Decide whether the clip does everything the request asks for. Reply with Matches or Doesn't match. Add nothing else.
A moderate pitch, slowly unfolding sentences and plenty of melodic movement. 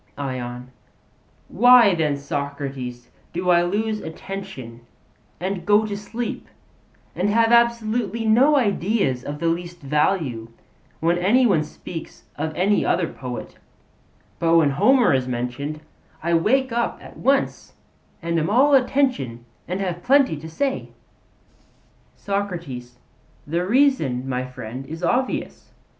Matches